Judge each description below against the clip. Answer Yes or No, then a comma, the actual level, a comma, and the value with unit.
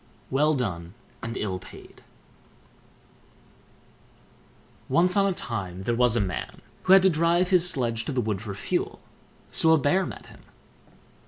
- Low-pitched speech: Yes, low, 125 Hz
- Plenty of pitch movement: Yes, wide, 8.3 semitones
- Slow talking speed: No, average, 155 wpm